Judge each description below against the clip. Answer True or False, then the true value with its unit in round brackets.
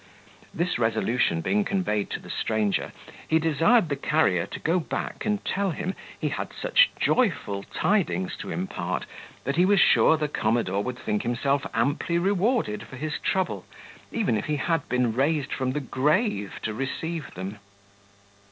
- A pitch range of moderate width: False (7.8 semitones)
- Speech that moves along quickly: False (160 wpm)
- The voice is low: False (150 Hz)